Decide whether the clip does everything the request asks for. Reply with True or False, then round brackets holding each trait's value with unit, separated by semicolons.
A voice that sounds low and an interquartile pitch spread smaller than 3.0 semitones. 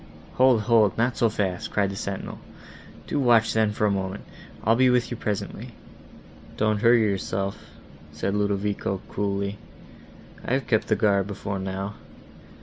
True (105 Hz; 2.5 semitones)